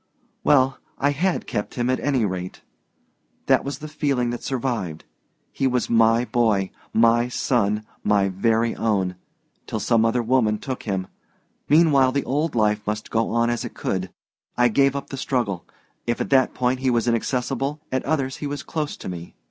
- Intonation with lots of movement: No, average, 3.7 semitones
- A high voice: No, low, 120 Hz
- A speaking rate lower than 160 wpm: No, average, 180 wpm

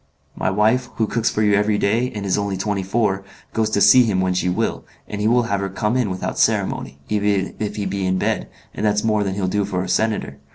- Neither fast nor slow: No, fast, 250 wpm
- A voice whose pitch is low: Yes, low, 105 Hz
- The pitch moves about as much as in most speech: No, narrow, 2.0 semitones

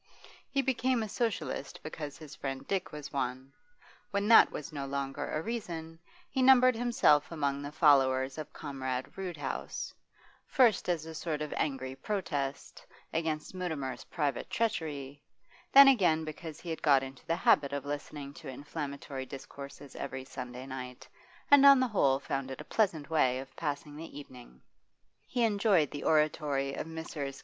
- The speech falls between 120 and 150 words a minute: No, average, 160 wpm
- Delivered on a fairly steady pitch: No, average, 4.2 semitones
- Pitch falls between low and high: Yes, medium, 150 Hz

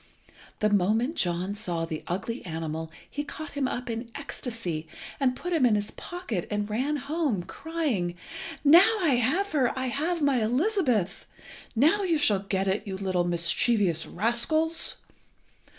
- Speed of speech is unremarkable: Yes, average, 150 wpm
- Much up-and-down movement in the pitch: Yes, wide, 7.7 semitones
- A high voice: Yes, high, 235 Hz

